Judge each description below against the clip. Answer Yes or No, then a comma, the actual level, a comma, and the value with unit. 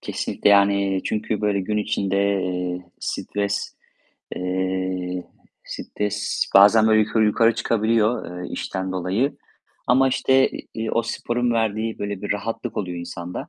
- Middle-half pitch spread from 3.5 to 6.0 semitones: No, average, 3.0 semitones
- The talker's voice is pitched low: Yes, low, 100 Hz